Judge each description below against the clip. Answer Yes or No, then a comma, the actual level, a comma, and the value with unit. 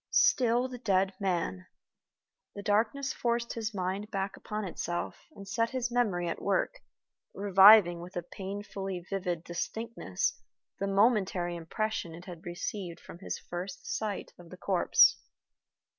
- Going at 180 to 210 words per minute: No, average, 140 wpm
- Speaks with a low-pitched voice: No, high, 195 Hz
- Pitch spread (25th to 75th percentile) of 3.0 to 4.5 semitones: Yes, average, 3.6 semitones